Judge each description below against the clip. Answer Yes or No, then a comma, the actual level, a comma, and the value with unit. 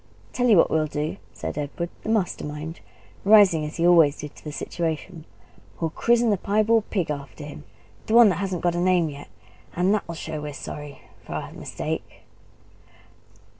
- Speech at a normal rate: Yes, average, 185 wpm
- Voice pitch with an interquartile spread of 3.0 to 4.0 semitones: No, average, 4.8 semitones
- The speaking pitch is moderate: Yes, medium, 170 Hz